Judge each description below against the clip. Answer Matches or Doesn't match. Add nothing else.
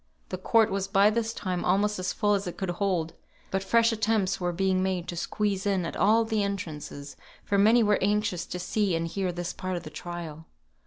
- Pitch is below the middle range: Doesn't match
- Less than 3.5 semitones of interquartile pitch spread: Matches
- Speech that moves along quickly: Matches